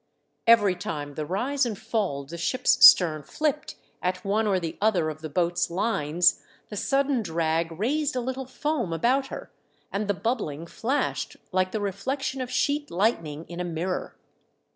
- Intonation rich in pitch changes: Yes, wide, 7.1 semitones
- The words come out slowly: No, average, 175 wpm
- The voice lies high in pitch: Yes, high, 200 Hz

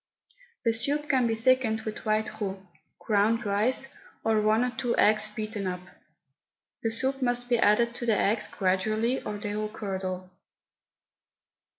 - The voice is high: Yes, high, 220 Hz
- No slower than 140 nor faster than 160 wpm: Yes, average, 155 wpm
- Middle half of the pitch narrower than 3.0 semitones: Yes, narrow, 2.4 semitones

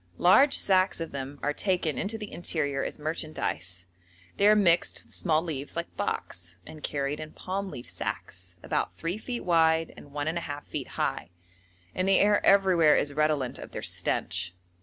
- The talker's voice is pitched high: No, medium, 160 Hz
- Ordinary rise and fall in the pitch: Yes, average, 4.6 semitones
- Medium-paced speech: Yes, average, 170 wpm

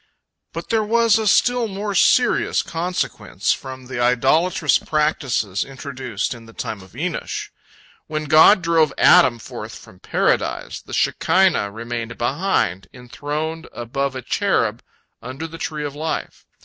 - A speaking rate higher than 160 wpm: No, slow, 135 wpm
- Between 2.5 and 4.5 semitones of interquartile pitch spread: No, wide, 5.6 semitones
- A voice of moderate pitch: Yes, medium, 145 Hz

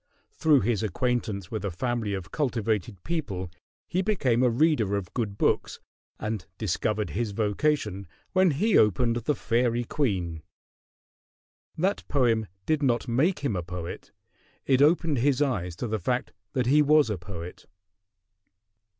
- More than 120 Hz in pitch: No, low, 115 Hz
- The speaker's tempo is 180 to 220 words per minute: No, average, 145 wpm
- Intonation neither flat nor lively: No, wide, 6.0 semitones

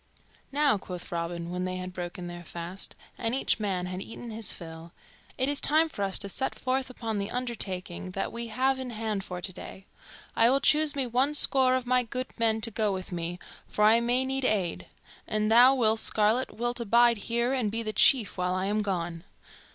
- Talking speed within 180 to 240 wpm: Yes, fast, 205 wpm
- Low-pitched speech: No, high, 220 Hz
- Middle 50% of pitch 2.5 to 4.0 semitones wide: No, average, 5.3 semitones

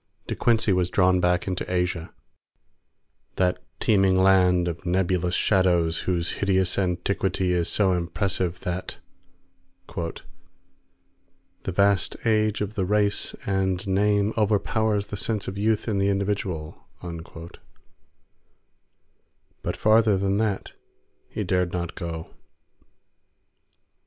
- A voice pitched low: Yes, very low, 95 Hz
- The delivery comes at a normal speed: No, slow, 110 wpm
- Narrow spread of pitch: Yes, narrow, 2.2 semitones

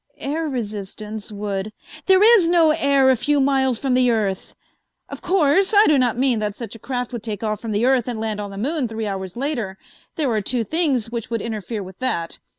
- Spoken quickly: Yes, fast, 225 wpm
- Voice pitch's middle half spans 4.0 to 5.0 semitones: Yes, average, 4.6 semitones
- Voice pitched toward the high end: Yes, high, 235 Hz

